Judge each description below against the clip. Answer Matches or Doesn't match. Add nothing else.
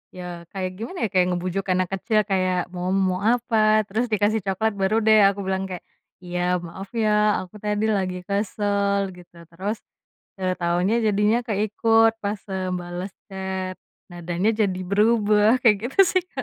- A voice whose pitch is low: Doesn't match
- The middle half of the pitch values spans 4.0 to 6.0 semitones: Doesn't match